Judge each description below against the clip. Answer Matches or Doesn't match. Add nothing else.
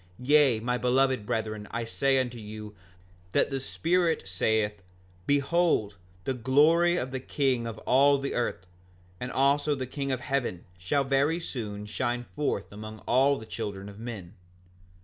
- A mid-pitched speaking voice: Doesn't match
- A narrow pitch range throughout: Doesn't match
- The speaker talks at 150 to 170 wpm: Matches